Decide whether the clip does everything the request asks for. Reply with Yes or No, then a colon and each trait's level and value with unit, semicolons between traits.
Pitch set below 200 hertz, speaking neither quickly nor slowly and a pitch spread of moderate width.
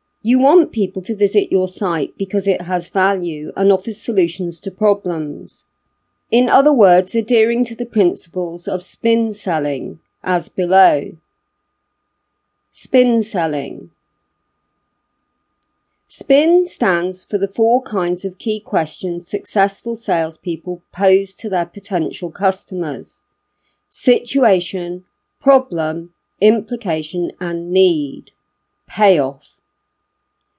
No: high, 190 Hz; slow, 100 wpm; average, 4.1 semitones